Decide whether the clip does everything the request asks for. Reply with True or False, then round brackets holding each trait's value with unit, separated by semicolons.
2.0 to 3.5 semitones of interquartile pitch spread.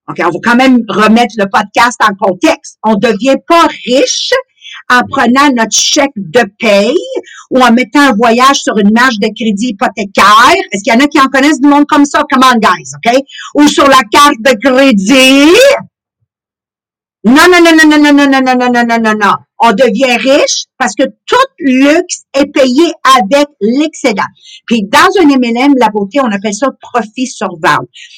False (4.3 semitones)